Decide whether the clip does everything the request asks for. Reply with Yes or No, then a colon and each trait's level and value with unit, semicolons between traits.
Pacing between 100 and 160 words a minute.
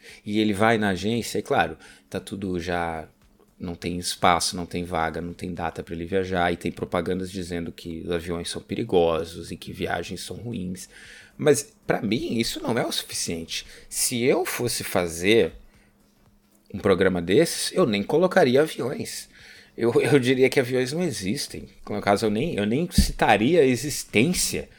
No: average, 170 wpm